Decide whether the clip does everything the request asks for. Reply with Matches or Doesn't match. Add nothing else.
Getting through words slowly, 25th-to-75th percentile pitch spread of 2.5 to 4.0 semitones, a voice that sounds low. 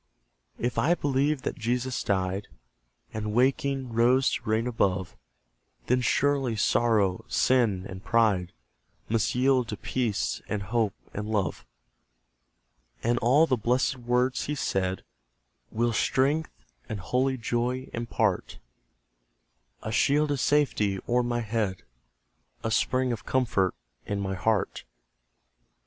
Matches